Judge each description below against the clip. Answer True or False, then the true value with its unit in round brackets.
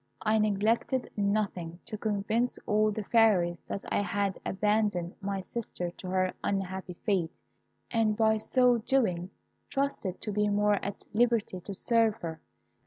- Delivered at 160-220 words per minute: False (145 wpm)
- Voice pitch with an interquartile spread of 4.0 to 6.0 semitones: False (2.7 semitones)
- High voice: True (205 Hz)